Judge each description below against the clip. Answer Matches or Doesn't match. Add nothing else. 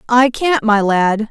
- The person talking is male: Doesn't match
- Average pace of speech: Matches